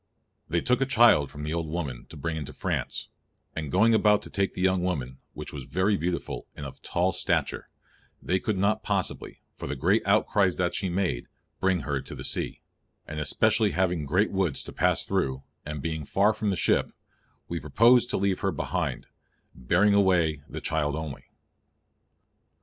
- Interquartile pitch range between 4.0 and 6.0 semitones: Yes, average, 4.7 semitones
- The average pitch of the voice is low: Yes, very low, 90 Hz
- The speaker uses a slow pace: No, average, 185 wpm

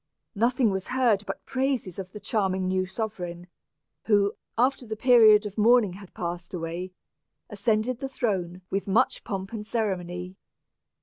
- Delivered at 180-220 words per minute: No, average, 145 wpm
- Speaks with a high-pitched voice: Yes, high, 205 Hz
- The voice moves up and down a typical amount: Yes, average, 3.7 semitones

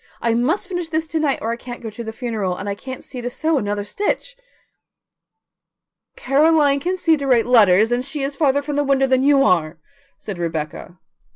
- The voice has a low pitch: No, very high, 260 Hz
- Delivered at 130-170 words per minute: No, fast, 205 wpm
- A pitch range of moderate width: Yes, average, 4.8 semitones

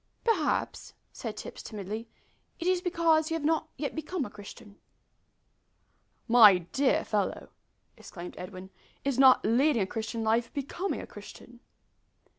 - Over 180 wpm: No, slow, 135 wpm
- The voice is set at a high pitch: Yes, high, 245 Hz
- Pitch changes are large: Yes, wide, 7.0 semitones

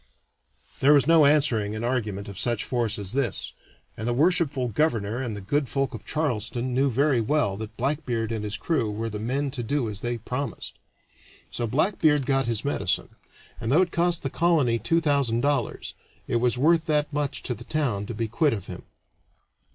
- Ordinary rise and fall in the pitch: Yes, average, 4.5 semitones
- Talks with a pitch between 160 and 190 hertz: No, low, 125 Hz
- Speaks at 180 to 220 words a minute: Yes, average, 195 wpm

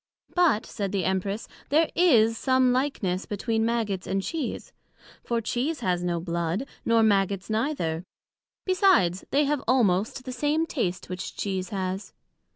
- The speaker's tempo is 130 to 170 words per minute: Yes, average, 145 wpm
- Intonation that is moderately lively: No, wide, 5.8 semitones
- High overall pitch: Yes, high, 220 Hz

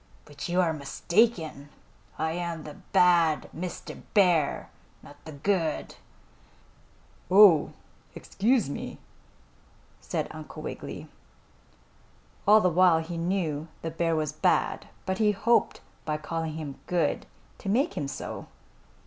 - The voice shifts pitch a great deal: No, average, 3.4 semitones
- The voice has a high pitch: No, medium, 165 Hz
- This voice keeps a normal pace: No, slow, 125 wpm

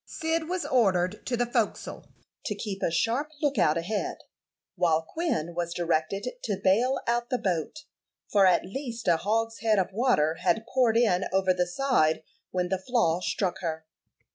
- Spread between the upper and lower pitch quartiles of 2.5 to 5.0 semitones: No, wide, 5.5 semitones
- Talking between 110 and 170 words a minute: Yes, average, 165 wpm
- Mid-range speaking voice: No, high, 195 Hz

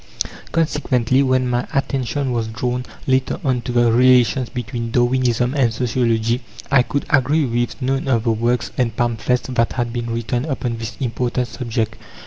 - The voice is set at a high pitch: No, low, 125 Hz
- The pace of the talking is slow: No, average, 160 wpm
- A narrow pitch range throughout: Yes, narrow, 1.8 semitones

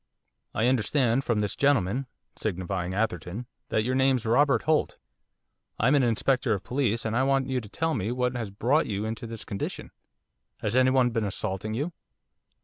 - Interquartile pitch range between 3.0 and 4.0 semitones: Yes, average, 3.7 semitones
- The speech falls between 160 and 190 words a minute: Yes, average, 175 wpm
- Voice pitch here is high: No, low, 115 Hz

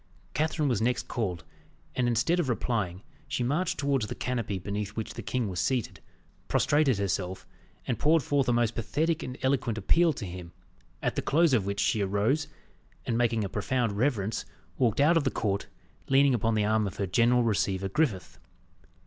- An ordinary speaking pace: Yes, average, 185 wpm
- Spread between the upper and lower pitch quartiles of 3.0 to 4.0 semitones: No, average, 5.0 semitones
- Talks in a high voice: No, low, 120 Hz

